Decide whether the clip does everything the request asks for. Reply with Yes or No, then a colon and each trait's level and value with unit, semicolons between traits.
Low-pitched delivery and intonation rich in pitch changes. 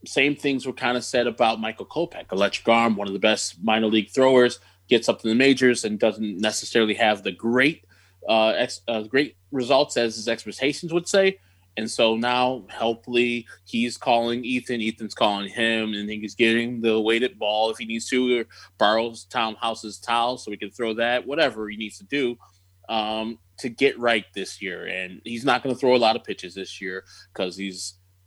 No: low, 110 Hz; average, 2.8 semitones